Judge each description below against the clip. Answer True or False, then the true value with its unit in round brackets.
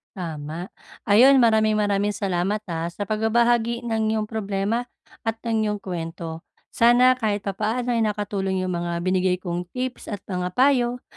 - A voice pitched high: True (210 Hz)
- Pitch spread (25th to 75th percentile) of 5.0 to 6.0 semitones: False (4.0 semitones)